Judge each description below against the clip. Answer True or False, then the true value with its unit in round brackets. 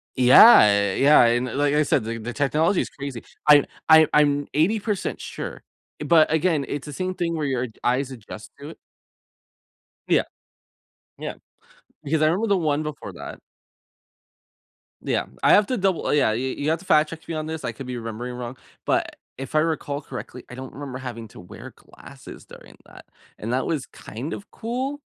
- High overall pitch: False (145 Hz)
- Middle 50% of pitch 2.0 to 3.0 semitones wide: False (4.2 semitones)